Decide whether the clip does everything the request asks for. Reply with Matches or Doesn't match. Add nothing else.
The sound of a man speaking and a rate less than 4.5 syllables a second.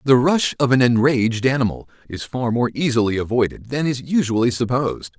Doesn't match